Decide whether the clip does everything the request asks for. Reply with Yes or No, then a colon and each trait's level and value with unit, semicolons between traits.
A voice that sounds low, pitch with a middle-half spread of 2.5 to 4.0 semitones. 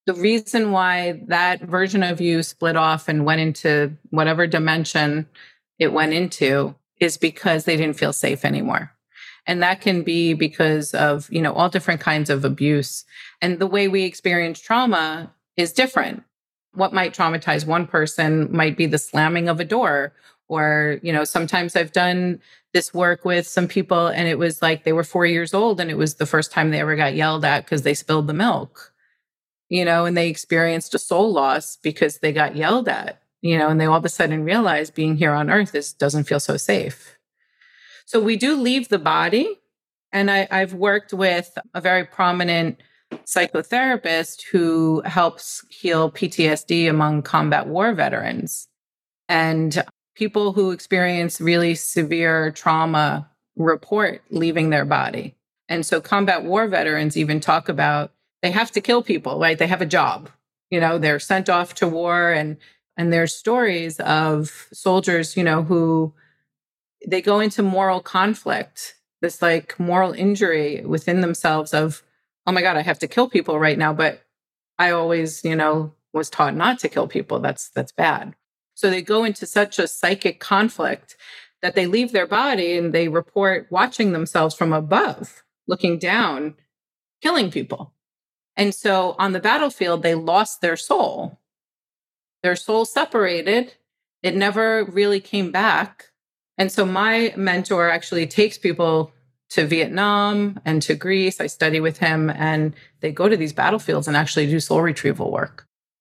No: medium, 170 Hz; average, 3.4 semitones